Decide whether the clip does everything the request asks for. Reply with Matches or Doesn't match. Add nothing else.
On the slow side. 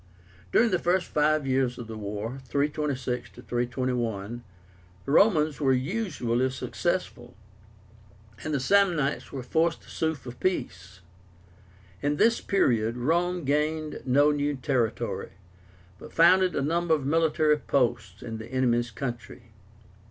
Matches